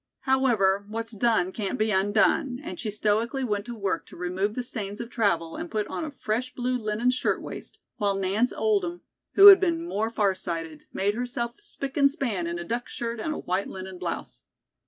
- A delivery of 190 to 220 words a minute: Yes, average, 200 wpm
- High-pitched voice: Yes, high, 220 Hz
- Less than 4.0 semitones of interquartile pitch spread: No, average, 4.3 semitones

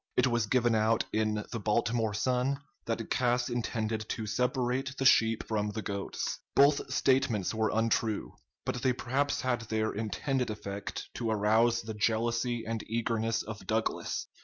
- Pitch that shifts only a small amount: Yes, narrow, 2.2 semitones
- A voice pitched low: Yes, low, 115 Hz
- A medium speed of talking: Yes, average, 155 wpm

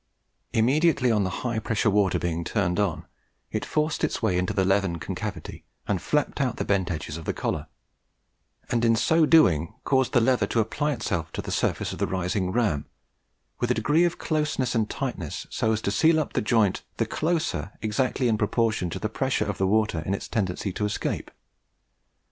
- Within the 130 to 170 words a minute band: No, average, 195 wpm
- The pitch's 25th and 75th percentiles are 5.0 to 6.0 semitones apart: Yes, average, 5.3 semitones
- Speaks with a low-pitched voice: Yes, low, 110 Hz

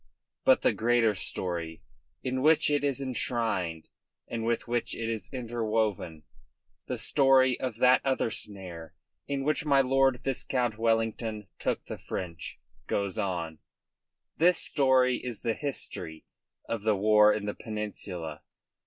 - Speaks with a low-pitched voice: Yes, low, 115 Hz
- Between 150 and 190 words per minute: No, slow, 135 wpm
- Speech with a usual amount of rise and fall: Yes, average, 4.4 semitones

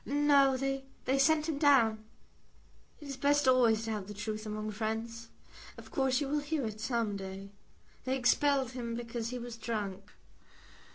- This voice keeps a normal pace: Yes, average, 165 wpm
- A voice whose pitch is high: Yes, high, 240 Hz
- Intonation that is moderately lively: Yes, average, 3.9 semitones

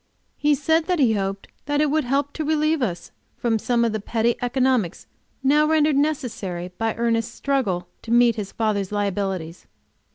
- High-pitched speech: Yes, high, 235 Hz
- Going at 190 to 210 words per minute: No, average, 165 wpm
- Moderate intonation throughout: No, wide, 5.7 semitones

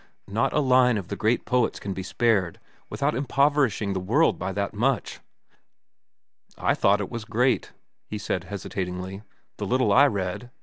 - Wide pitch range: No, average, 4.6 semitones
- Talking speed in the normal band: Yes, average, 165 wpm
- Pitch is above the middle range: No, low, 110 Hz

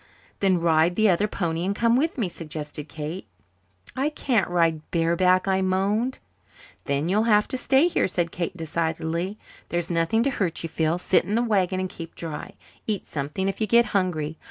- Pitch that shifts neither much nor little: Yes, average, 4.2 semitones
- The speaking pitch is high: No, medium, 180 Hz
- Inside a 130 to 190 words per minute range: Yes, average, 185 wpm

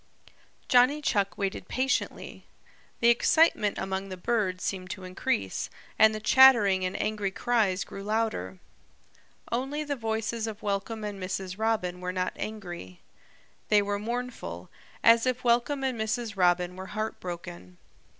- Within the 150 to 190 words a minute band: No, average, 140 wpm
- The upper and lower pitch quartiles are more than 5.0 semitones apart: No, average, 4.1 semitones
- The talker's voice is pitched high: Yes, high, 210 Hz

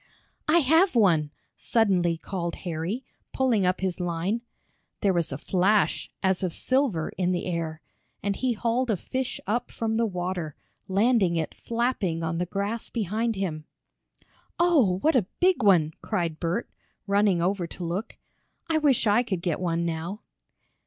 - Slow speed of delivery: No, average, 160 wpm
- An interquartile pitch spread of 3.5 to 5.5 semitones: Yes, average, 5.2 semitones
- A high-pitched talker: Yes, high, 195 Hz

